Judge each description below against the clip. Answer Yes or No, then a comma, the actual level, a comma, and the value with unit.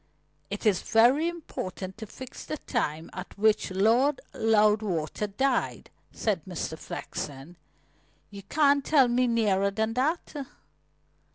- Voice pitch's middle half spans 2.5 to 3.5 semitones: No, average, 5.1 semitones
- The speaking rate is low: Yes, slow, 120 wpm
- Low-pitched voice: No, high, 220 Hz